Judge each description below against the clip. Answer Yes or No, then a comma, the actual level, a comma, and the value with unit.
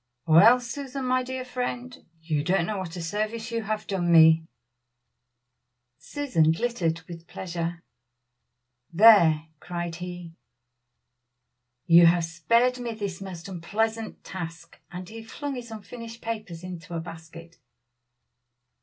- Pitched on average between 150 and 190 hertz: Yes, medium, 185 Hz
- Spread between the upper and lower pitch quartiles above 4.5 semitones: Yes, wide, 5.6 semitones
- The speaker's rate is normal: No, slow, 125 wpm